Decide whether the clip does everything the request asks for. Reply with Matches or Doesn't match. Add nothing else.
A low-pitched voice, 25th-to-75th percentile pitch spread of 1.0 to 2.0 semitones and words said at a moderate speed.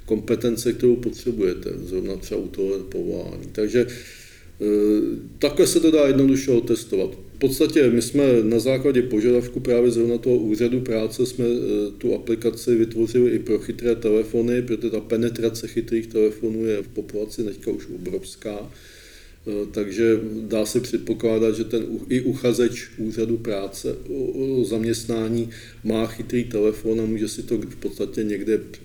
Matches